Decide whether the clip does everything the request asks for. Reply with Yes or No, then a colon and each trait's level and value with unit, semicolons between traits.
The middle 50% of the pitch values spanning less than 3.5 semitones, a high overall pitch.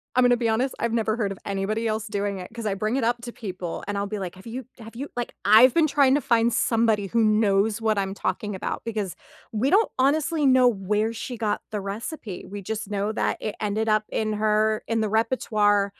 Yes: narrow, 2.5 semitones; high, 220 Hz